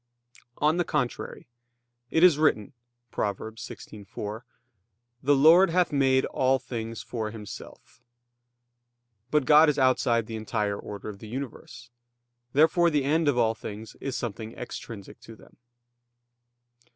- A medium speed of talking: No, slow, 130 wpm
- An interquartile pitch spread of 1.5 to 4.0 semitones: No, average, 5.1 semitones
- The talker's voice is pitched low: Yes, low, 125 Hz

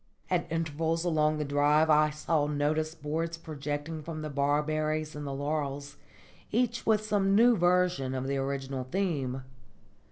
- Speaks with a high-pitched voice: No, medium, 155 Hz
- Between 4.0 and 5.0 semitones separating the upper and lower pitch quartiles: No, narrow, 2.4 semitones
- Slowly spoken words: No, average, 150 wpm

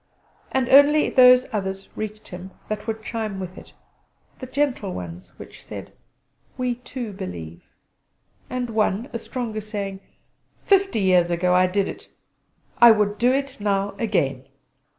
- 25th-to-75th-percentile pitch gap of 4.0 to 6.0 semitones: Yes, average, 4.7 semitones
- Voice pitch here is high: Yes, high, 215 Hz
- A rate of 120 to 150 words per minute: Yes, average, 145 wpm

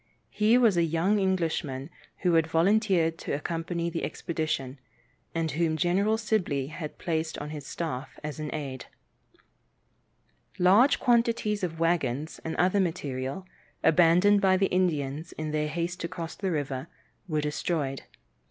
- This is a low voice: No, medium, 165 Hz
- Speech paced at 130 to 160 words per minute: Yes, average, 145 wpm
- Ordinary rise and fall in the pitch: Yes, average, 3.5 semitones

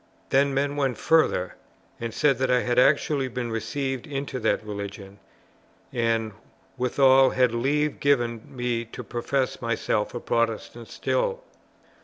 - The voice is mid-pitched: No, low, 125 Hz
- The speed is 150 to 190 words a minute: No, slow, 135 wpm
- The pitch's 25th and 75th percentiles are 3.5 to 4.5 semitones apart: No, average, 3.1 semitones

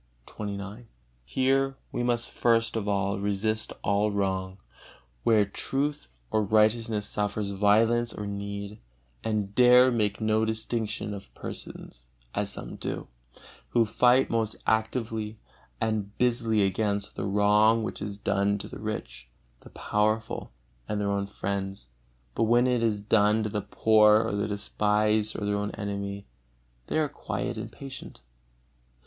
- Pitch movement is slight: Yes, narrow, 1.9 semitones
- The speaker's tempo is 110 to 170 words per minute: Yes, average, 140 wpm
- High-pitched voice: No, low, 105 Hz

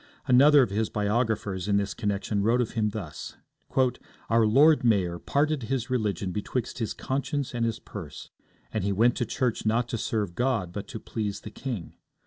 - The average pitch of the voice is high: No, low, 110 Hz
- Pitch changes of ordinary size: Yes, average, 3.6 semitones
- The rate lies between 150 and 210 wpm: Yes, average, 180 wpm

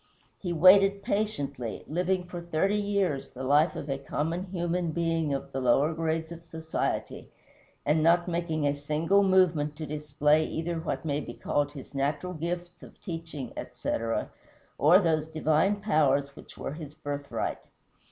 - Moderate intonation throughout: Yes, average, 3.2 semitones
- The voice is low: No, medium, 160 Hz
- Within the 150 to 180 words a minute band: Yes, average, 155 wpm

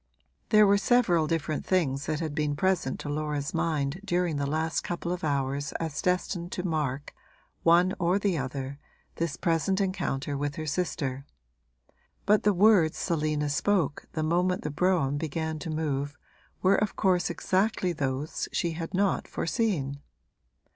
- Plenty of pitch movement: No, average, 3.9 semitones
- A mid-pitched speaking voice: Yes, medium, 160 Hz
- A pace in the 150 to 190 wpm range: Yes, average, 155 wpm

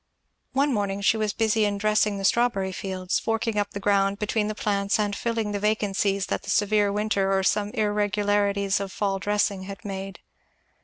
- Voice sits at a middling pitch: No, high, 205 Hz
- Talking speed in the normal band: Yes, average, 185 wpm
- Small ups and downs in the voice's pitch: Yes, narrow, 1.3 semitones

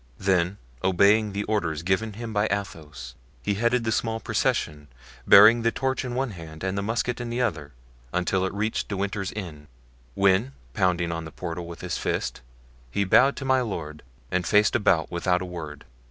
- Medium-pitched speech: No, very low, 95 Hz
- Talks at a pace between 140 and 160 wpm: No, average, 185 wpm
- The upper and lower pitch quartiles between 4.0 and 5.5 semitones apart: Yes, average, 4.6 semitones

